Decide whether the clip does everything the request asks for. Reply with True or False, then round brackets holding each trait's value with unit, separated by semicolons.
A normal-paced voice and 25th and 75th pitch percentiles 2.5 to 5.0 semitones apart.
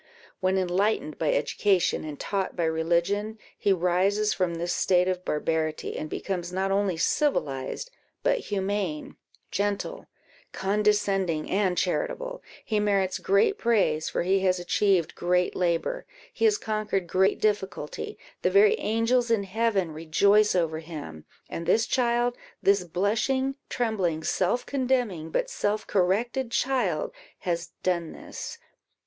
False (130 wpm; 4.0 semitones)